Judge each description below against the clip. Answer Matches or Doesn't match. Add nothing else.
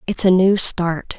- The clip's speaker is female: Matches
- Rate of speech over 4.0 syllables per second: Doesn't match